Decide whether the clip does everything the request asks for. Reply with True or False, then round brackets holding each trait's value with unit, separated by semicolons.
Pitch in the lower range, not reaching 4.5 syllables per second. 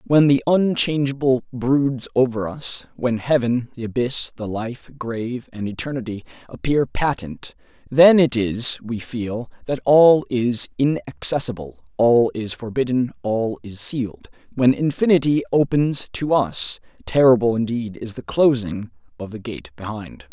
True (125 Hz; 4.2 syllables/s)